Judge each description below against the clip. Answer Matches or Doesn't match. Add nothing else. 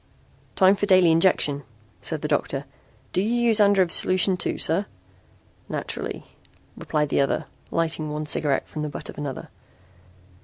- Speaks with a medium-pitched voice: Matches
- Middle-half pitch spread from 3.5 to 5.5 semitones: Matches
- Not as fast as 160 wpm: Matches